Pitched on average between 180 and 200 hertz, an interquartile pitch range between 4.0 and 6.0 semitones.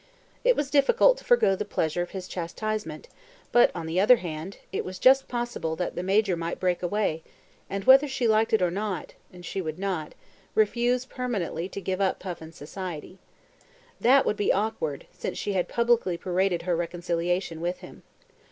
Yes: high, 190 Hz; average, 4.3 semitones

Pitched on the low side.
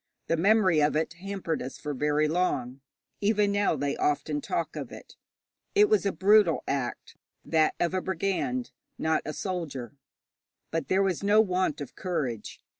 No: medium, 165 Hz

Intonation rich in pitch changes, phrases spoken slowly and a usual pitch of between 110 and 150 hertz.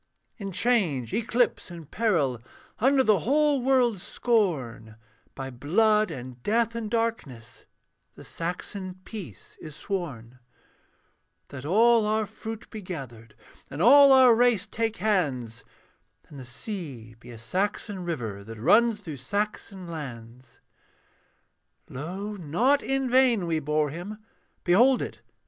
No: wide, 9.0 semitones; slow, 125 wpm; medium, 185 Hz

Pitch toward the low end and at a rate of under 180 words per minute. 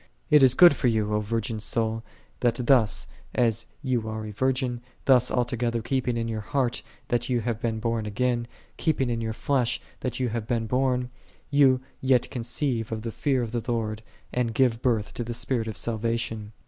No: low, 120 Hz; average, 190 wpm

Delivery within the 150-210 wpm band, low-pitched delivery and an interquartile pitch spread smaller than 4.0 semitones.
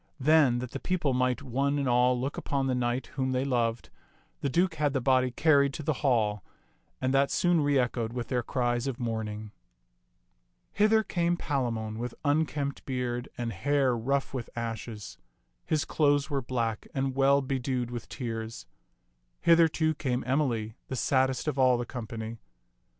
Yes: average, 165 wpm; low, 130 Hz; average, 2.8 semitones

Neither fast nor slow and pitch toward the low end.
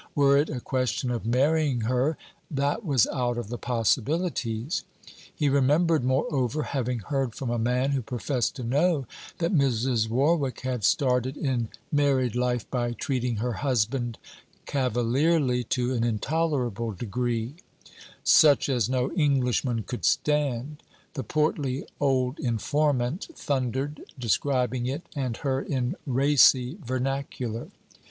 No: slow, 130 wpm; low, 130 Hz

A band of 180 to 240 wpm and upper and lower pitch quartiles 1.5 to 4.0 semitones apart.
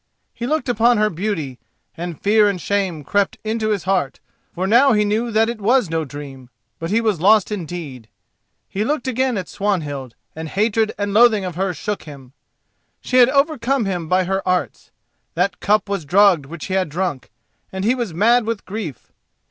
No: average, 190 wpm; average, 4.6 semitones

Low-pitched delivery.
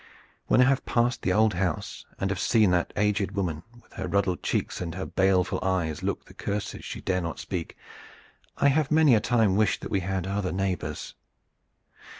Yes: very low, 95 Hz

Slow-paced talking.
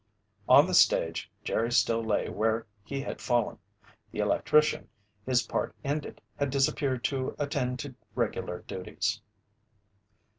Yes: slow, 125 wpm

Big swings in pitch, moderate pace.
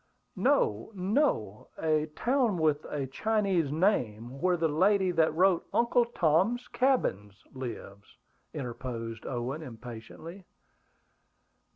No: wide, 8.1 semitones; slow, 100 wpm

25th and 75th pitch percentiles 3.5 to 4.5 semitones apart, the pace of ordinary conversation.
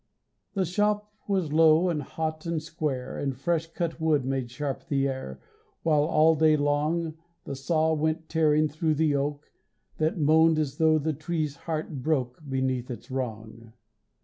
No: average, 2.8 semitones; average, 160 wpm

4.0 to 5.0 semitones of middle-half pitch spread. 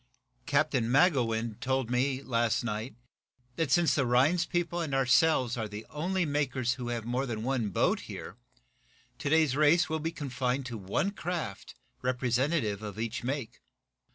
Yes: average, 4.4 semitones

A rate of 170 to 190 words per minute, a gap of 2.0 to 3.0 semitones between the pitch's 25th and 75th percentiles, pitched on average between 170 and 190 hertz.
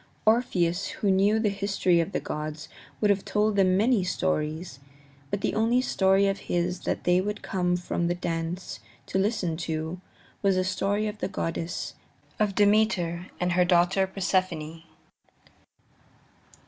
No: average, 150 wpm; average, 2.7 semitones; medium, 185 Hz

